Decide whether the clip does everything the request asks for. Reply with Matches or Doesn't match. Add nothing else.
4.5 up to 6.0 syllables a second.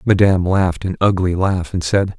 Matches